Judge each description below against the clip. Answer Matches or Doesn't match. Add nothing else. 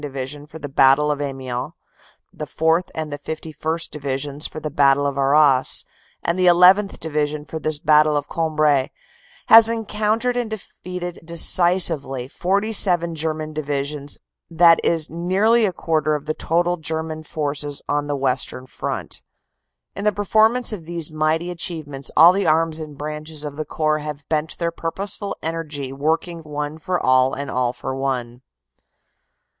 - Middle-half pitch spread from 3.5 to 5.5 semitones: Doesn't match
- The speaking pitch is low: Doesn't match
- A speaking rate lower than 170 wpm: Matches